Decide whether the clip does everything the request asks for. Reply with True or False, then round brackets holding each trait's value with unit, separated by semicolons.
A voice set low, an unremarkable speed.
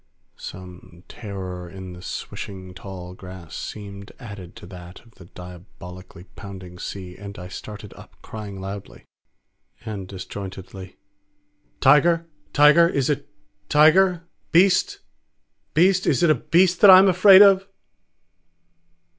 False (100 Hz; 125 wpm)